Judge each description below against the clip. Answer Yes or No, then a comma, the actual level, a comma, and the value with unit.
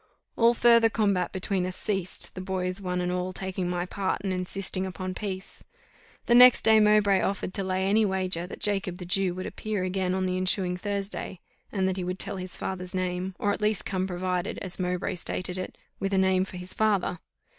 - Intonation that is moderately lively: No, narrow, 1.5 semitones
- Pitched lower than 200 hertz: Yes, medium, 185 Hz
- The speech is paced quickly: Yes, fast, 210 wpm